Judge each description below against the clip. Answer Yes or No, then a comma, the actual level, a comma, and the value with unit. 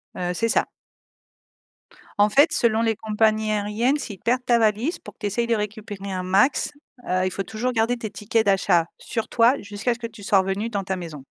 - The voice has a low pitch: No, high, 215 Hz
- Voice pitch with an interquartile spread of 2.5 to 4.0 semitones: Yes, average, 2.9 semitones